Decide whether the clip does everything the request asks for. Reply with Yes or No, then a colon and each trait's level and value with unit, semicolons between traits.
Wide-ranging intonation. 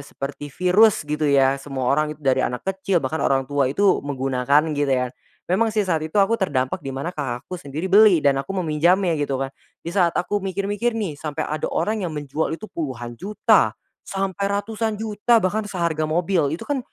Yes: wide, 5.9 semitones